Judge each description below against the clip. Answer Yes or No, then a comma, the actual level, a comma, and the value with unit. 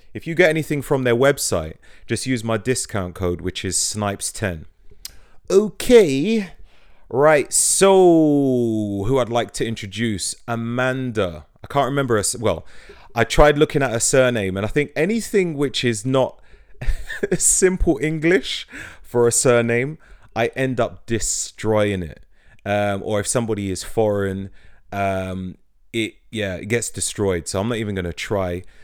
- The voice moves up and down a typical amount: No, wide, 5.7 semitones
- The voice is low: Yes, low, 115 Hz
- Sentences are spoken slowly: No, average, 145 wpm